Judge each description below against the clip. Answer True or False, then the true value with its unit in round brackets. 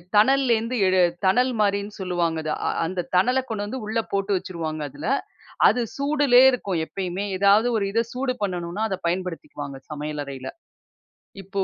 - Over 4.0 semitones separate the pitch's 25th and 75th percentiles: True (4.9 semitones)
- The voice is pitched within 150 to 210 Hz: True (200 Hz)